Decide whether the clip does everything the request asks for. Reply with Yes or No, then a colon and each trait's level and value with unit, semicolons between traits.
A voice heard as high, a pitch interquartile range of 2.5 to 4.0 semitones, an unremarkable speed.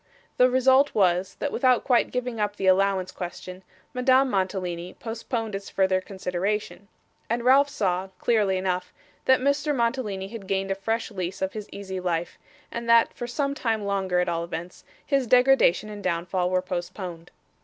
No: high, 200 Hz; average, 4.7 semitones; average, 165 wpm